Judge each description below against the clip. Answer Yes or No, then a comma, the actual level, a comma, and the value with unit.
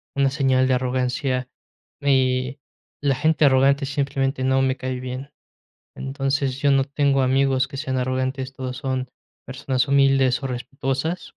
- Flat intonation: Yes, narrow, 1.1 semitones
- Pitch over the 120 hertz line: Yes, low, 135 Hz